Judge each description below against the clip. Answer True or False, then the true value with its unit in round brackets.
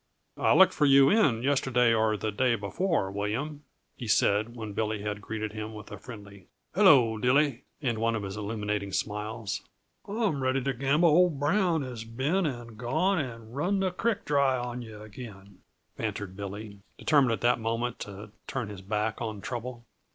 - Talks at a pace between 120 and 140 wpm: False (175 wpm)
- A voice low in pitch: True (115 Hz)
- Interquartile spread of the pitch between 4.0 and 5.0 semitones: True (4.7 semitones)